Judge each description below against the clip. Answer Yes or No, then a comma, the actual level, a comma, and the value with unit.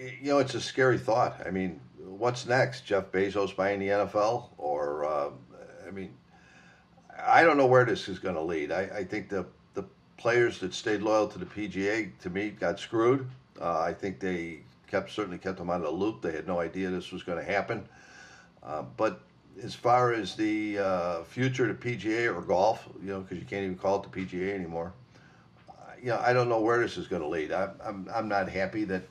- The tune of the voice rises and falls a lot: No, average, 4.0 semitones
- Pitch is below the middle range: Yes, low, 100 Hz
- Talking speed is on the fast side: Yes, fast, 220 wpm